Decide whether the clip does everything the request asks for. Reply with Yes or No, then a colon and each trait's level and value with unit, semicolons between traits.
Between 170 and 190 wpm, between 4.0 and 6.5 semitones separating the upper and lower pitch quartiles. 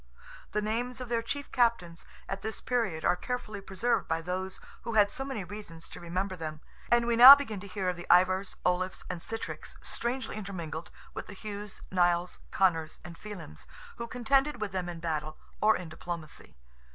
Yes: average, 185 wpm; average, 4.7 semitones